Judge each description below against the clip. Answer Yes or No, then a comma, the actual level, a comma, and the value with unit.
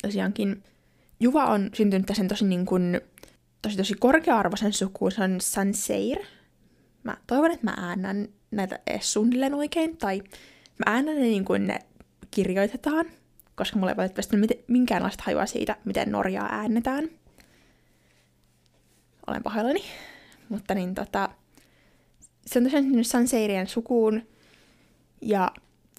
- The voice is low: No, high, 215 Hz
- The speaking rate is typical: Yes, average, 120 wpm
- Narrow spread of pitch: No, average, 4.1 semitones